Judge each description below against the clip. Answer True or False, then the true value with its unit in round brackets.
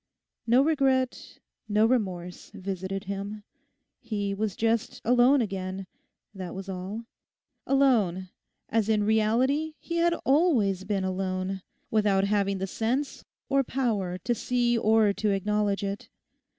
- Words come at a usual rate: False (125 wpm)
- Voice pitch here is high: True (210 Hz)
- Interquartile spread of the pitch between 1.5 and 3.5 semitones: False (3.9 semitones)